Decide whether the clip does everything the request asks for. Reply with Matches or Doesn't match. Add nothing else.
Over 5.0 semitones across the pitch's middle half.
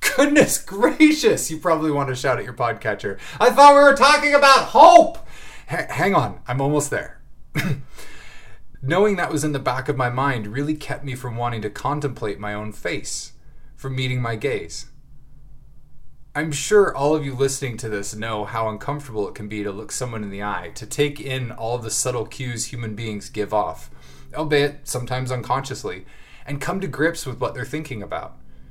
Matches